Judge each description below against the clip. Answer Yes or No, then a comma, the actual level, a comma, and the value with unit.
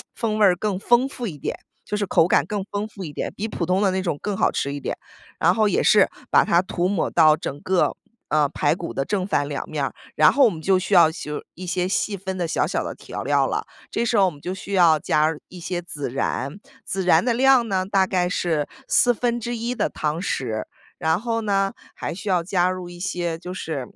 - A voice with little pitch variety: No, average, 4.1 semitones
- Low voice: No, medium, 185 Hz